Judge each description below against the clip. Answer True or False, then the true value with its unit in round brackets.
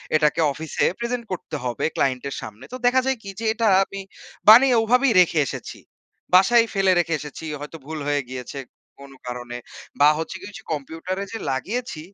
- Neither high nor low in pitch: True (165 Hz)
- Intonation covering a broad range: True (7.9 semitones)